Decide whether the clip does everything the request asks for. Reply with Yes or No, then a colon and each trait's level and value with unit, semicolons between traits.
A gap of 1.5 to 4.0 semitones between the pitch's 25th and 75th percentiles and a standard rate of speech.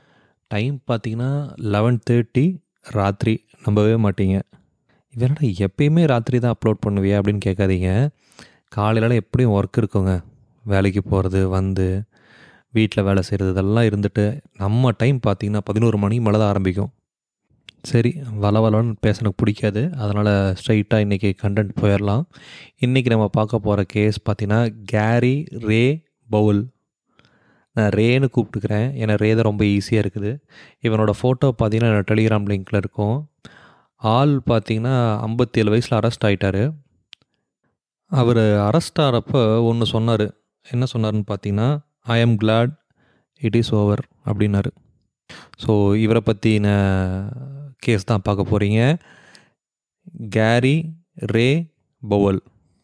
No: average, 3.1 semitones; slow, 115 wpm